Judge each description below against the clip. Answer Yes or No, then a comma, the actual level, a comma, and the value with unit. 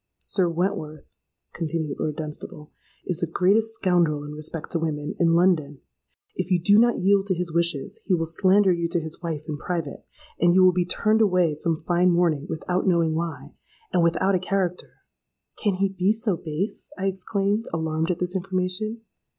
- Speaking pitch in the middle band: Yes, medium, 175 Hz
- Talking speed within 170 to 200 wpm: Yes, average, 180 wpm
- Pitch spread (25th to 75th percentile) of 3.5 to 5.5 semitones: No, average, 2.9 semitones